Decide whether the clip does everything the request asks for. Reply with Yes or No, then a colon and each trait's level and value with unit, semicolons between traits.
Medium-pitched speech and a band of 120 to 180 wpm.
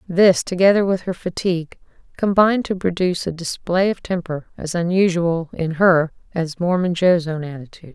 Yes: medium, 175 Hz; average, 160 wpm